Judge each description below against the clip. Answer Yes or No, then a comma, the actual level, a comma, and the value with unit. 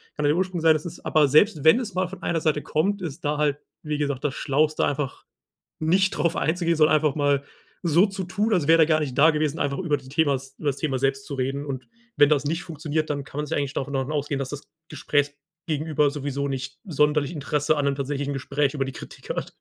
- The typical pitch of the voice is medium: Yes, medium, 150 Hz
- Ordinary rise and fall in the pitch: No, narrow, 2.3 semitones